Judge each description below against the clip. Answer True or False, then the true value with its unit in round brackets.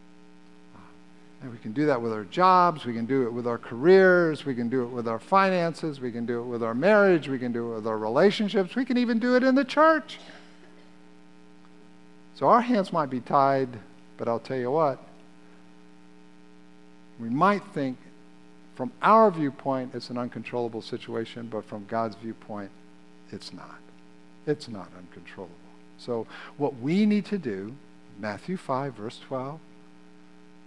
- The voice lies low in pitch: True (115 Hz)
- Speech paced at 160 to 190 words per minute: True (165 wpm)